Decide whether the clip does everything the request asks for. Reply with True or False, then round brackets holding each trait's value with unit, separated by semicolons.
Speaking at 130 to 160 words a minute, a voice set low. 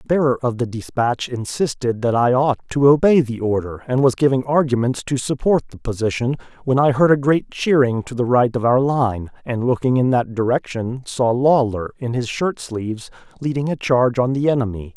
False (200 wpm; 125 Hz)